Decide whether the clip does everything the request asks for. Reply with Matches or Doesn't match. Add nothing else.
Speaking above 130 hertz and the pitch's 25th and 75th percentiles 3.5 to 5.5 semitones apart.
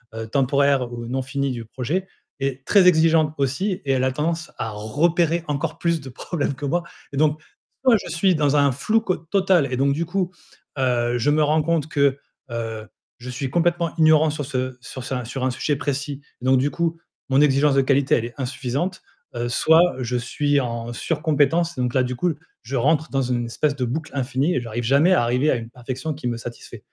Matches